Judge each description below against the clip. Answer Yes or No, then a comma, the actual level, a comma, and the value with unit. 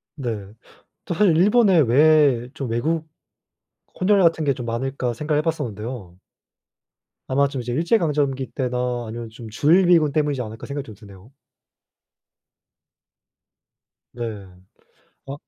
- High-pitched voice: No, low, 135 Hz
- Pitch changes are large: No, average, 5.0 semitones